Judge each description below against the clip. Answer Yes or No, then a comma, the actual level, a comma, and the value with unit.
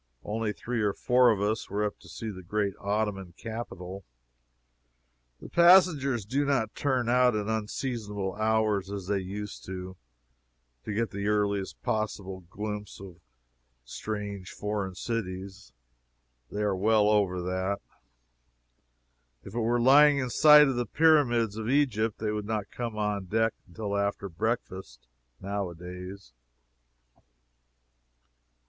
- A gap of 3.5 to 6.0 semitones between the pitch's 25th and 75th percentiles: No, average, 2.9 semitones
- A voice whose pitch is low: Yes, low, 105 Hz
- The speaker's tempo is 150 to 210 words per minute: No, slow, 135 wpm